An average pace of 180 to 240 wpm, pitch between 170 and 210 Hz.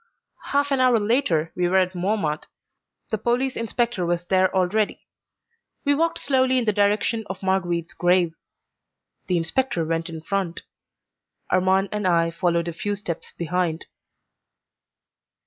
No: average, 140 wpm; high, 190 Hz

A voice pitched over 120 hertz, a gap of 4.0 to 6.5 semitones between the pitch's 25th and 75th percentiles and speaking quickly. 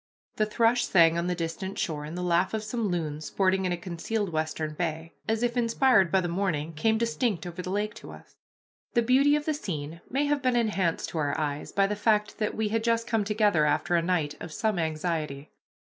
Yes: high, 190 Hz; average, 5.2 semitones; fast, 220 wpm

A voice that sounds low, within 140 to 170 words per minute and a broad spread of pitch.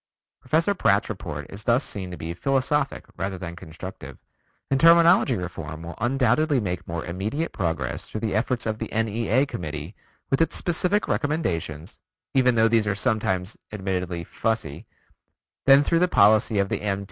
Yes: low, 110 Hz; average, 160 wpm; wide, 6.8 semitones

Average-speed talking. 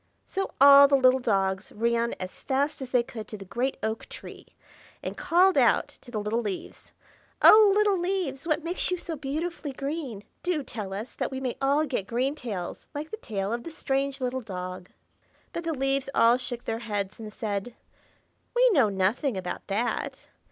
Yes: average, 185 wpm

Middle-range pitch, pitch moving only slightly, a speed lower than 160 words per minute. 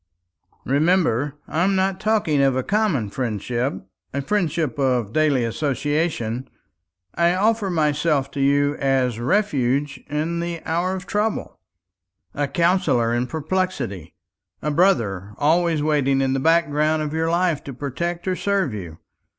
No: medium, 150 Hz; average, 4.7 semitones; average, 140 wpm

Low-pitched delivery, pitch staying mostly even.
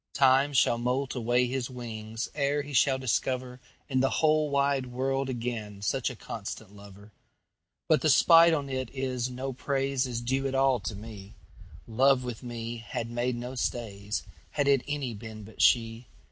No: low, 125 Hz; average, 3.0 semitones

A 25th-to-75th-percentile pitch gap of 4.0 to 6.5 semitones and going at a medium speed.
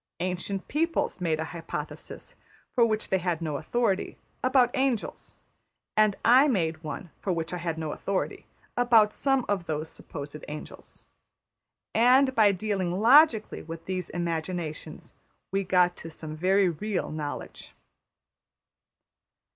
No: average, 5.2 semitones; slow, 130 wpm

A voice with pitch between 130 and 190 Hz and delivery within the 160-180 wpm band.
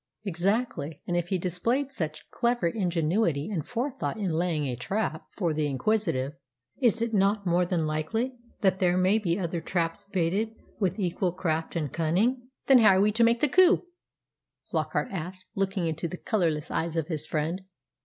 Yes: medium, 185 Hz; average, 175 wpm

